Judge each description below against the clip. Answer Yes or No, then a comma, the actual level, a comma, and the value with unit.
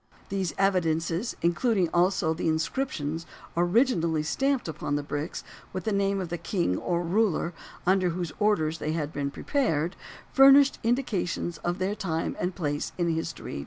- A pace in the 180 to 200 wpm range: No, average, 155 wpm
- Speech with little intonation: No, average, 3.6 semitones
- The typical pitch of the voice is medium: Yes, medium, 175 Hz